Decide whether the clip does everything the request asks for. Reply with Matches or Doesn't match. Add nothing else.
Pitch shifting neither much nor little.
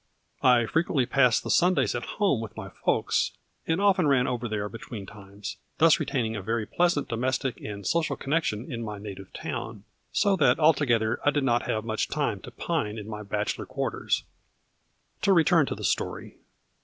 Doesn't match